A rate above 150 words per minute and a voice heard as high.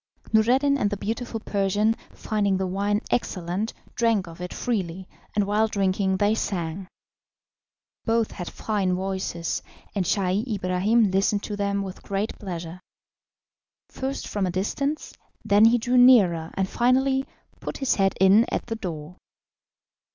No: average, 145 wpm; high, 200 Hz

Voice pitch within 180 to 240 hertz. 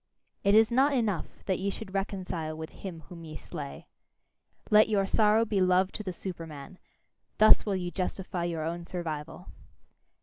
Yes: medium, 185 Hz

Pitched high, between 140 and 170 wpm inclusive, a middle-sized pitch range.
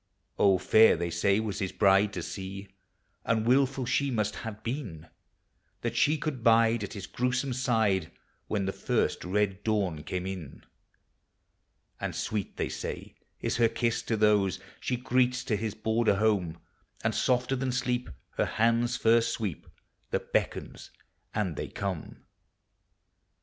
No: low, 110 Hz; average, 150 wpm; average, 3.6 semitones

